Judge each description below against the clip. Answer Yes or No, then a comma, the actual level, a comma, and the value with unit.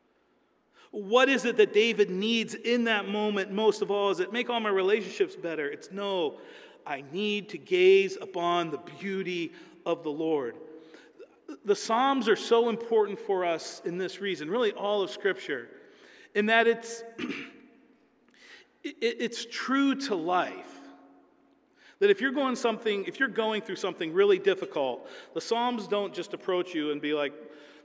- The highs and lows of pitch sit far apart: Yes, wide, 5.7 semitones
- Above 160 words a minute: No, average, 155 wpm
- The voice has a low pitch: No, high, 225 Hz